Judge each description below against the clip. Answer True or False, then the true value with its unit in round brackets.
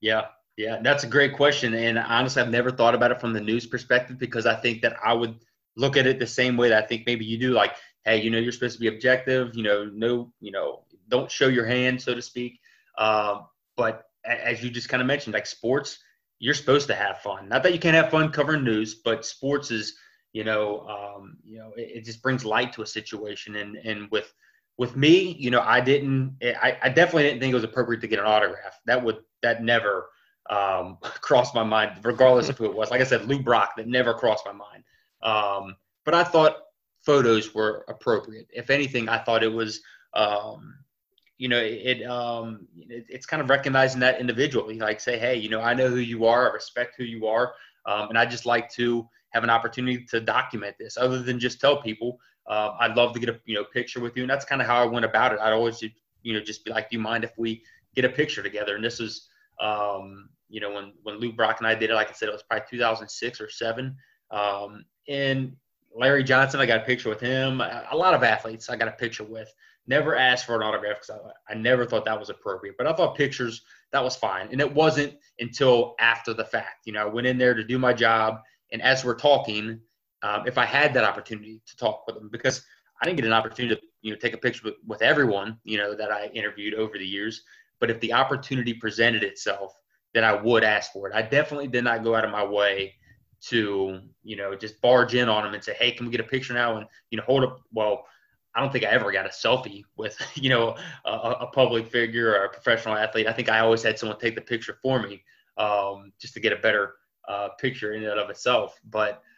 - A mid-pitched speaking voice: False (115 Hz)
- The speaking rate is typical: False (240 wpm)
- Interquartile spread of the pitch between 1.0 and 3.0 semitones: True (2.5 semitones)